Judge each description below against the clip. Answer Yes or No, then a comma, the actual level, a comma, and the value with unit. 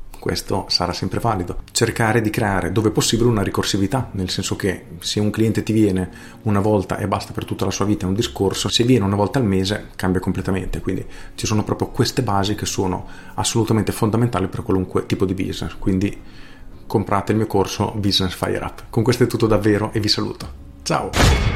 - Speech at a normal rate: No, fast, 200 wpm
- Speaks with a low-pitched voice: Yes, low, 100 Hz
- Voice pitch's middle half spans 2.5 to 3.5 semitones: Yes, average, 2.8 semitones